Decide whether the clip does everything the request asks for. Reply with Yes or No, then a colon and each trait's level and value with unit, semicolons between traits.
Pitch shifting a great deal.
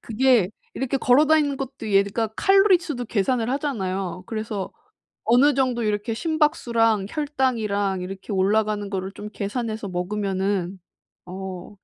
No: average, 5.0 semitones